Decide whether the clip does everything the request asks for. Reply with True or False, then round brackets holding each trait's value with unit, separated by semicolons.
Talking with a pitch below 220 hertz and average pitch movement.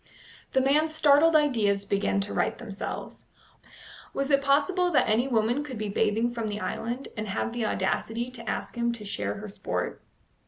False (235 Hz; 4.6 semitones)